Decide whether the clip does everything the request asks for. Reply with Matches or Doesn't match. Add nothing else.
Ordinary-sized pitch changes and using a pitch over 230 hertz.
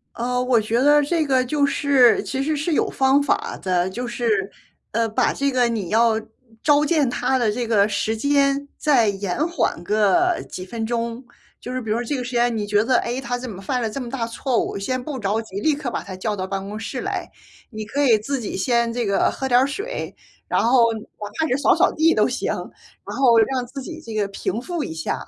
Matches